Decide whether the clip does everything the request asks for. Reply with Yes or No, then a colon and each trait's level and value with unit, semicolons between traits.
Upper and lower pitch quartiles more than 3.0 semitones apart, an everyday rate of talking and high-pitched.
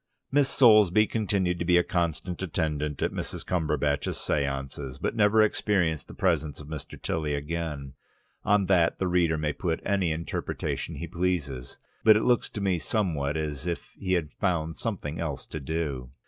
No: average, 4.1 semitones; average, 165 wpm; very low, 85 Hz